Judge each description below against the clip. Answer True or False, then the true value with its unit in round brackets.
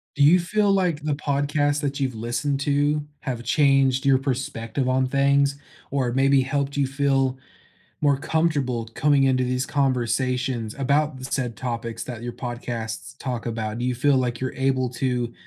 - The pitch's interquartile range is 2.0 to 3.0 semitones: True (2.4 semitones)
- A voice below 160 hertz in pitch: True (135 Hz)